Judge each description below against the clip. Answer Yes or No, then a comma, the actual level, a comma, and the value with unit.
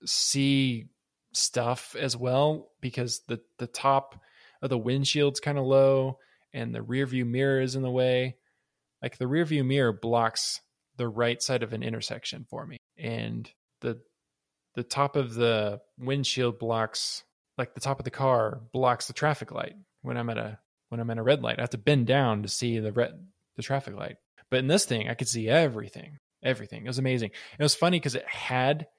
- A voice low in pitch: Yes, low, 130 Hz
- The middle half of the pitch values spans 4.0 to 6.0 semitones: No, average, 2.7 semitones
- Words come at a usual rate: Yes, average, 195 wpm